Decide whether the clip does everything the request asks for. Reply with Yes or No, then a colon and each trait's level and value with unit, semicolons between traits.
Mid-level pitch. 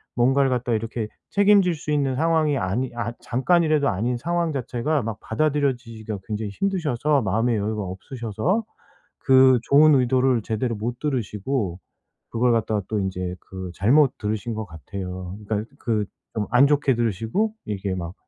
No: low, 120 Hz